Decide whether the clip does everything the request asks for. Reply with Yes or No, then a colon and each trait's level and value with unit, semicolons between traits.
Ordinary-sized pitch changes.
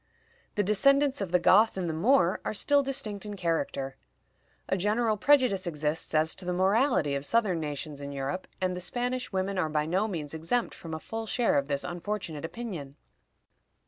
No: wide, 5.7 semitones